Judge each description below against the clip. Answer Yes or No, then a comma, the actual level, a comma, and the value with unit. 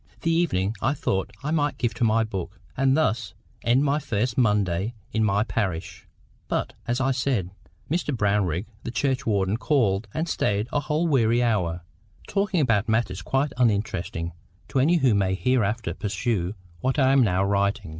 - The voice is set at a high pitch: No, low, 115 Hz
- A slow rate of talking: No, average, 165 wpm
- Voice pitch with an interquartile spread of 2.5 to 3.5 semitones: No, average, 5.2 semitones